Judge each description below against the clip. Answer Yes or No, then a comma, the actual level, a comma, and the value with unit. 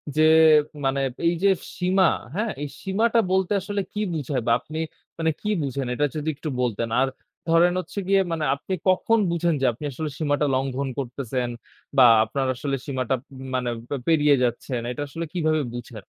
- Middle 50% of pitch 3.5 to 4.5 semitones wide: No, average, 5.0 semitones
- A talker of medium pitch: Yes, medium, 150 Hz